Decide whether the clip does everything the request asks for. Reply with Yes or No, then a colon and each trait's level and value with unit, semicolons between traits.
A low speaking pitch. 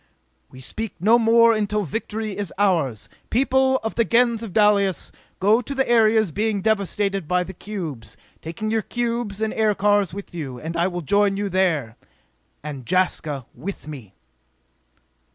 No: high, 200 Hz